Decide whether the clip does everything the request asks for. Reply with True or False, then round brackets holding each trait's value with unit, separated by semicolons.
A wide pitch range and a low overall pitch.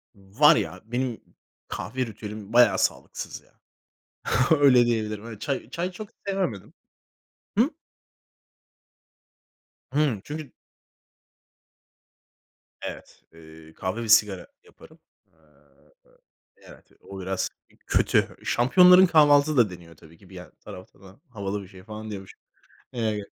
True (5.9 semitones; 110 Hz)